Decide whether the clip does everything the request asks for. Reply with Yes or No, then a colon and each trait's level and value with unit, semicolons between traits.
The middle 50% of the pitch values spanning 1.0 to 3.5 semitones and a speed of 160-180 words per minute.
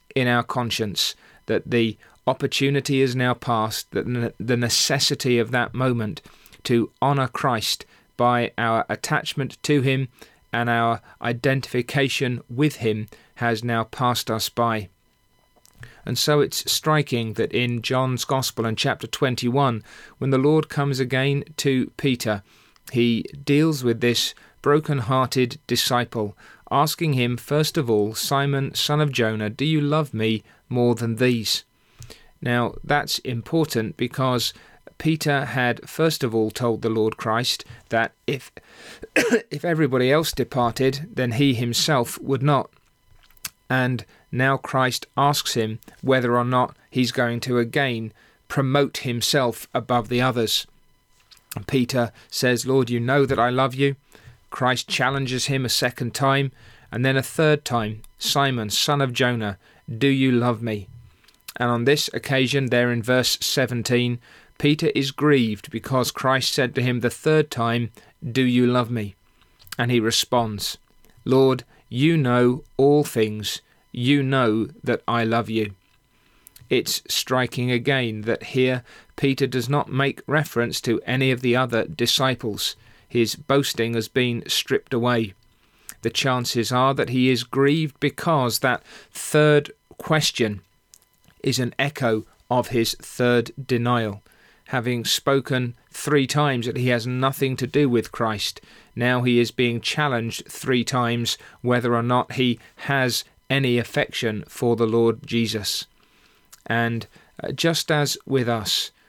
No: average, 2.8 semitones; average, 140 wpm